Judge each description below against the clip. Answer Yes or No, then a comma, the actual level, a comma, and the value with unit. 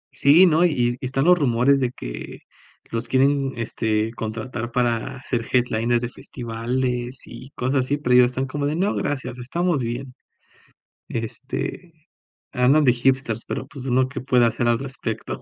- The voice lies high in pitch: No, low, 125 Hz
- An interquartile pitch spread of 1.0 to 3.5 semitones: Yes, narrow, 2.5 semitones